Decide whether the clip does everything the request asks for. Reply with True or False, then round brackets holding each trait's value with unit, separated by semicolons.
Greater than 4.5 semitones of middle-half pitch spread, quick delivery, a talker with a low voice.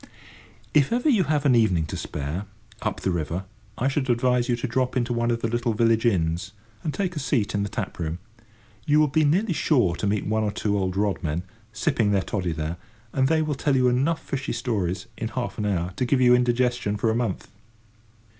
True (5.1 semitones; 220 wpm; 120 Hz)